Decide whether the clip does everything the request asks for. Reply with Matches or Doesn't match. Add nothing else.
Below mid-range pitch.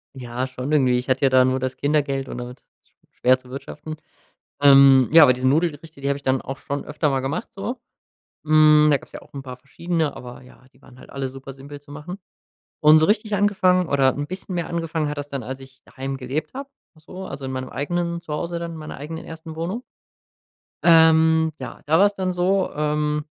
Doesn't match